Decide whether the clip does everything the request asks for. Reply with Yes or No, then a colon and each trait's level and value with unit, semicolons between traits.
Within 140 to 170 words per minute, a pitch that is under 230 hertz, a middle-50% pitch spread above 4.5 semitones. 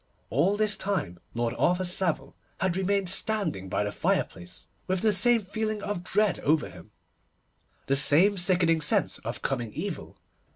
Yes: average, 155 wpm; medium, 185 Hz; wide, 5.4 semitones